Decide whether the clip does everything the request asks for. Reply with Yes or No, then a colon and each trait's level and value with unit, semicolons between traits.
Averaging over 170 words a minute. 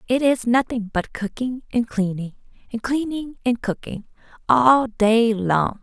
No: average, 145 wpm